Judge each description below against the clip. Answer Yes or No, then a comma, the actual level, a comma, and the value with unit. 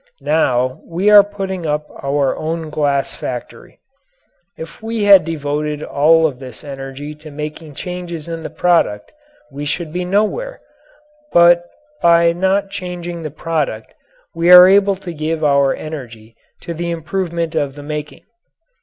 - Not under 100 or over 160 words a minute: Yes, average, 145 wpm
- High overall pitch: No, medium, 160 Hz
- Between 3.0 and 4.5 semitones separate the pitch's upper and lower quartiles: Yes, average, 3.5 semitones